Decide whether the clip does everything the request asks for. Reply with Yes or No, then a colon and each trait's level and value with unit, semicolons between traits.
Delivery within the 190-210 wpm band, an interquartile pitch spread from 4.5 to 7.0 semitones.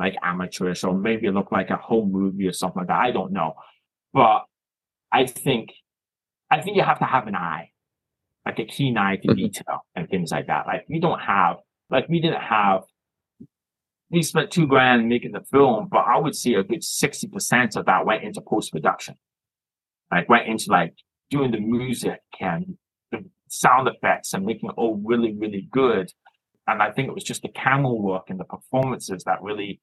Yes: average, 195 wpm; average, 5.1 semitones